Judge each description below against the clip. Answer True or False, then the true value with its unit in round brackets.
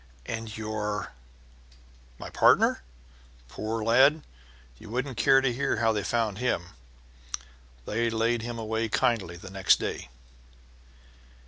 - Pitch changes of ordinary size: True (3.3 semitones)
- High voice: False (110 Hz)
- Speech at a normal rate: False (125 wpm)